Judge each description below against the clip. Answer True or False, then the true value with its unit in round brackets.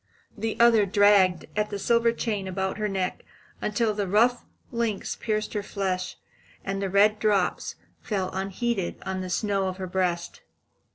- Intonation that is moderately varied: False (2.1 semitones)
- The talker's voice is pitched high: True (200 Hz)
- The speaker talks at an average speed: True (160 wpm)